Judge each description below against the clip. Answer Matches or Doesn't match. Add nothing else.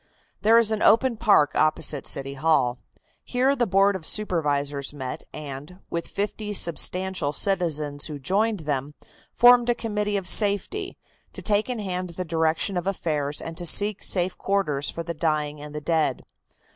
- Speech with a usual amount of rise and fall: Doesn't match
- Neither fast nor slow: Matches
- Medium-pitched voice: Matches